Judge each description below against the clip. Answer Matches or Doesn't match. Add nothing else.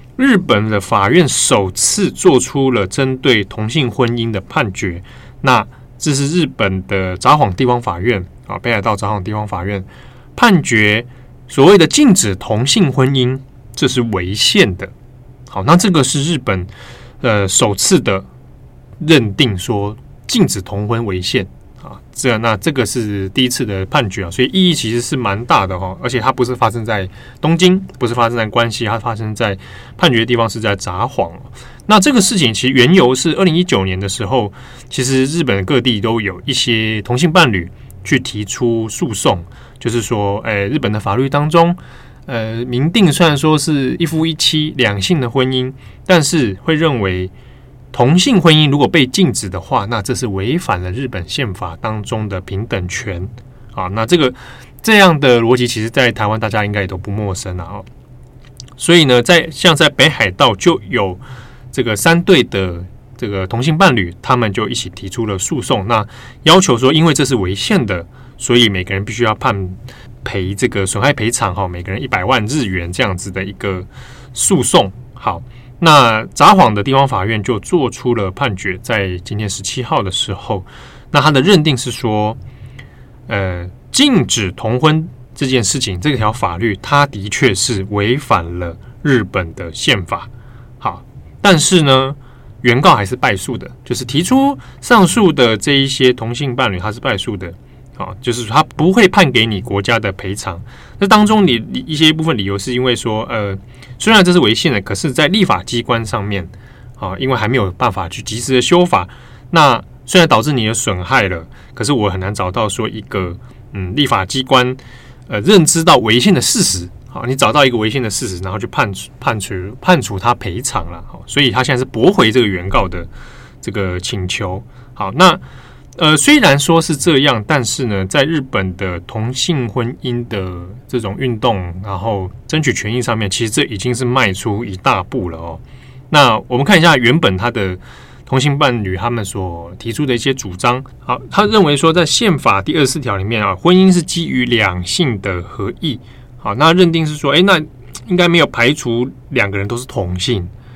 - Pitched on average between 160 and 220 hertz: Doesn't match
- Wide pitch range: Doesn't match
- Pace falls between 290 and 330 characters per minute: Doesn't match